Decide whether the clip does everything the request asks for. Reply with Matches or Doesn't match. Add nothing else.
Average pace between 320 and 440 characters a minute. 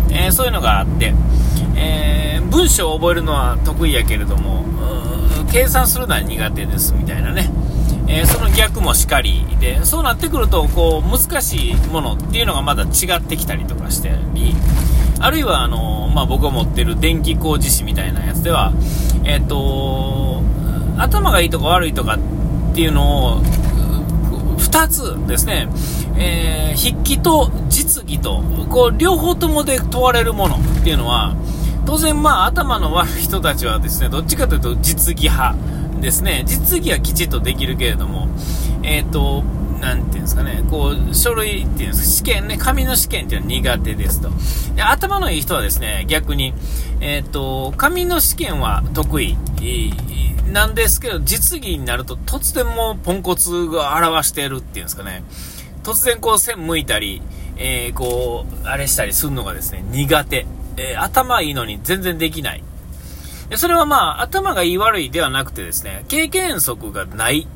Matches